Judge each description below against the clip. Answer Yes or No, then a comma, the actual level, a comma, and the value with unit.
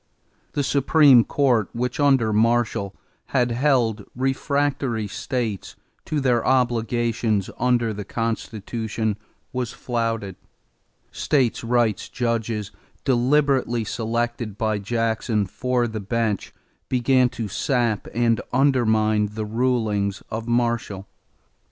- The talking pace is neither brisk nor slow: No, slow, 100 wpm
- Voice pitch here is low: Yes, low, 115 Hz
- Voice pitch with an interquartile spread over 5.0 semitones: No, narrow, 2.5 semitones